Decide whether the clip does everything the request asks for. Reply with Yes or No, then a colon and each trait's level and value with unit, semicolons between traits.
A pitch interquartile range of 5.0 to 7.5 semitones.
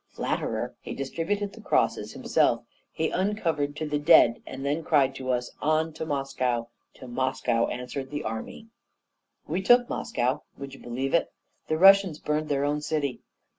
No: average, 3.7 semitones